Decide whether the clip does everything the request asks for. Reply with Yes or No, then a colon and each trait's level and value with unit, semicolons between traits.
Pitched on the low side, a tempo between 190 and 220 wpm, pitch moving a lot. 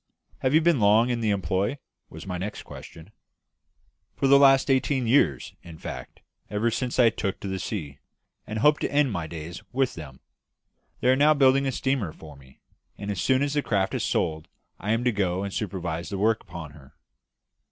Yes: low, 105 Hz; fast, 205 wpm; wide, 7.1 semitones